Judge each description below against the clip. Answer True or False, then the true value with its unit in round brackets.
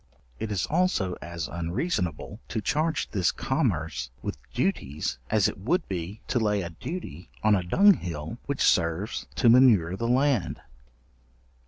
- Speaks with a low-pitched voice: True (105 Hz)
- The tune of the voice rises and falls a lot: True (7.2 semitones)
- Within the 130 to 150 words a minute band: True (145 wpm)